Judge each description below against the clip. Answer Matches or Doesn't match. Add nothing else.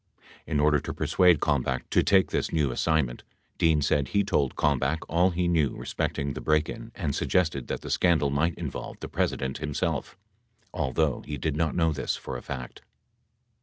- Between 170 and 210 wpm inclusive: Matches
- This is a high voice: Doesn't match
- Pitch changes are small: Doesn't match